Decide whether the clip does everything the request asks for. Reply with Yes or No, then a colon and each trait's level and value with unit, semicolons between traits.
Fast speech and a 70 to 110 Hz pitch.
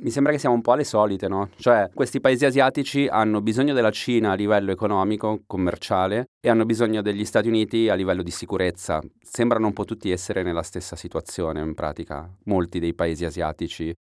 Yes: fast, 190 wpm; low, 105 Hz